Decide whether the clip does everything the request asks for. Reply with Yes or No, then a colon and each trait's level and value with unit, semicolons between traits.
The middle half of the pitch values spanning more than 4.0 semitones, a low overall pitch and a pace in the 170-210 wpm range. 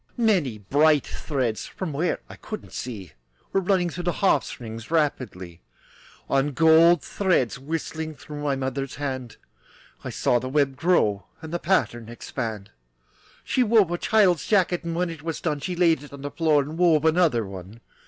No: average, 5.1 semitones; medium, 150 Hz; average, 175 wpm